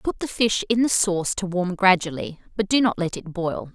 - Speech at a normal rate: No, fast, 240 wpm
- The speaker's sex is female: Yes, female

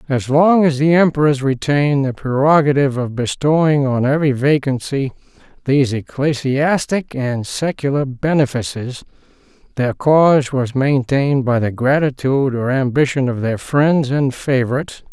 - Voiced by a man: Yes, male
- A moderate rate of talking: No, slow, 125 wpm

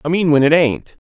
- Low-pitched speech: No, medium, 155 Hz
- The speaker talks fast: Yes, fast, 280 wpm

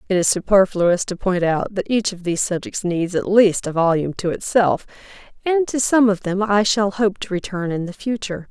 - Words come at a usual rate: No, fast, 220 wpm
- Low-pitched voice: No, high, 195 Hz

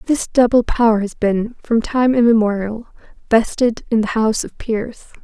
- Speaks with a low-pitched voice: No, high, 225 Hz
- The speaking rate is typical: Yes, average, 160 wpm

